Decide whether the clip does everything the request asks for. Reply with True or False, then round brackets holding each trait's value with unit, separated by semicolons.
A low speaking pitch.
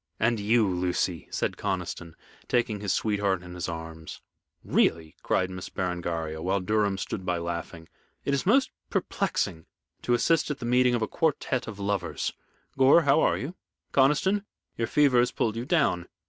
True (105 Hz)